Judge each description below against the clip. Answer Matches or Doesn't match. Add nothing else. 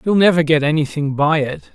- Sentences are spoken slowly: Doesn't match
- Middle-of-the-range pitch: Matches